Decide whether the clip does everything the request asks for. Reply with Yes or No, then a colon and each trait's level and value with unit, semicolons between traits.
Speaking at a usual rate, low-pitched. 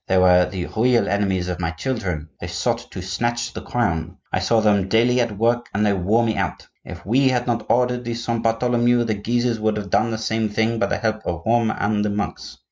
No: fast, 230 wpm; low, 110 Hz